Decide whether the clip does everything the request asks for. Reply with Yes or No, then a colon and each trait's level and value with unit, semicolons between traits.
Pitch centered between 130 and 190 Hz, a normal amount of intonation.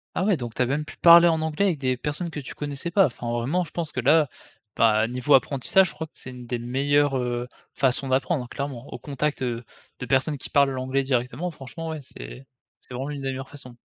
Yes: low, 135 Hz; average, 3.2 semitones